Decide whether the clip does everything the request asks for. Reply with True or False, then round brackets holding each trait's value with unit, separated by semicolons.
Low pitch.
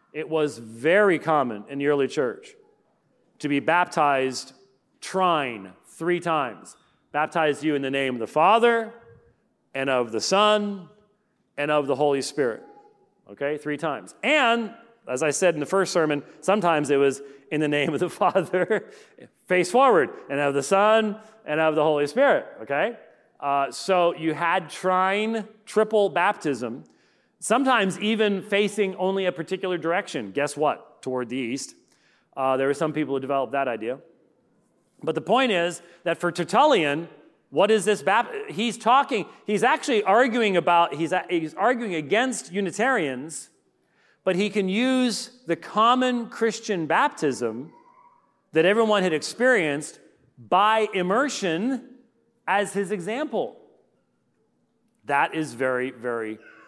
False (175 Hz)